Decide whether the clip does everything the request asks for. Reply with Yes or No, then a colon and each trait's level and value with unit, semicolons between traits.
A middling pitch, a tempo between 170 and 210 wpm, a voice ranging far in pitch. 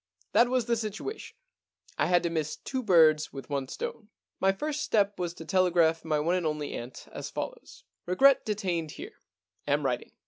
Yes: medium, 180 Hz; average, 195 wpm; wide, 6.0 semitones